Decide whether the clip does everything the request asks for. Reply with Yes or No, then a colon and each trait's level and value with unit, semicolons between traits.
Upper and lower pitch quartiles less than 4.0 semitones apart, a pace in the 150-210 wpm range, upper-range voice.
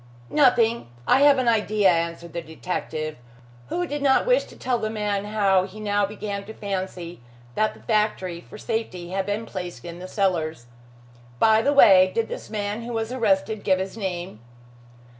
Yes: average, 3.3 semitones; average, 180 wpm; high, 205 Hz